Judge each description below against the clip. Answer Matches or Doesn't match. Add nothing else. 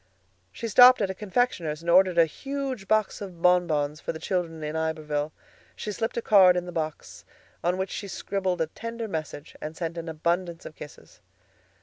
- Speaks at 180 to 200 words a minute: Matches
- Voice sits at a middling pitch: Matches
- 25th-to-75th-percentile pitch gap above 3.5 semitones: Matches